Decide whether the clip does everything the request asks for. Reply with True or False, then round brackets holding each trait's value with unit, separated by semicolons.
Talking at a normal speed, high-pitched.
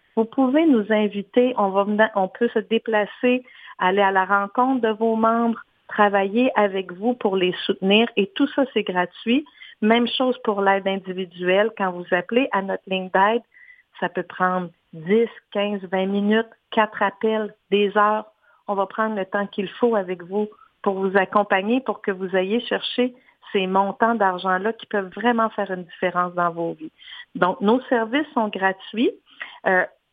True (175 wpm; 210 Hz)